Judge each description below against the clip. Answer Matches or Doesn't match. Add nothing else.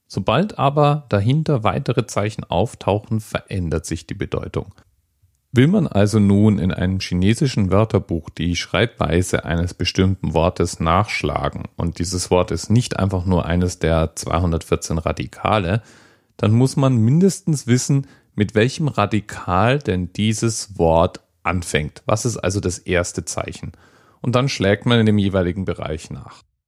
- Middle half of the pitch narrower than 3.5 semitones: Doesn't match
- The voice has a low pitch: Matches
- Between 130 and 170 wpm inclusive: Matches